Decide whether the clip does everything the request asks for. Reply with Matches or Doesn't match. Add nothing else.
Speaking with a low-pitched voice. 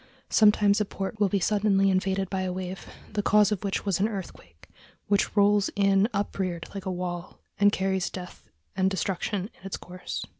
Doesn't match